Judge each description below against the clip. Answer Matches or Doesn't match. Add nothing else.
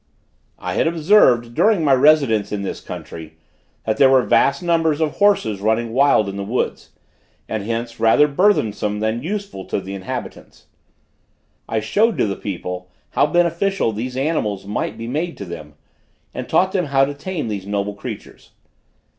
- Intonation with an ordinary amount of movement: Doesn't match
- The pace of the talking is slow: Doesn't match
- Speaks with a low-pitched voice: Matches